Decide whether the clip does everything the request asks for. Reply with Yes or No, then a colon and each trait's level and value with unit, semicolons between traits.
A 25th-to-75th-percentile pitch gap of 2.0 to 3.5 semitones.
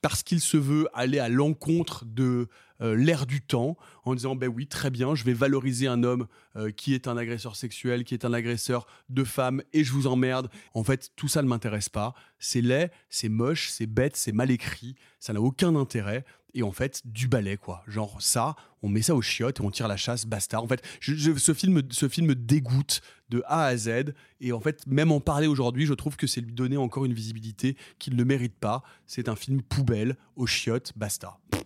Yes: average, 3.1 semitones